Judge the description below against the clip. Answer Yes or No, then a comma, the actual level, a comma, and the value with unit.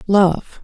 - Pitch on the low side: No, high, 195 Hz